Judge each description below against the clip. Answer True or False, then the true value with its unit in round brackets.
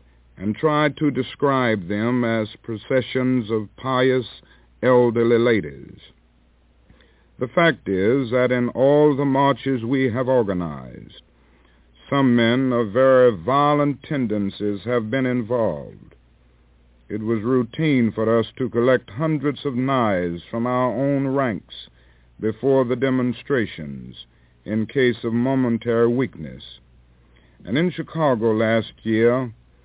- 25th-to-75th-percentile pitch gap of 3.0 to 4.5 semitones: False (5.1 semitones)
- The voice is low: True (120 Hz)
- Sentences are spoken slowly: True (115 wpm)